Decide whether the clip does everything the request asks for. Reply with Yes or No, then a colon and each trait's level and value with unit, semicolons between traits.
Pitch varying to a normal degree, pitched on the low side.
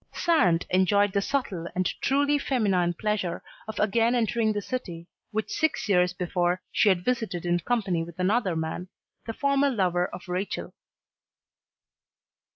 No: average, 4.6 semitones; high, 195 Hz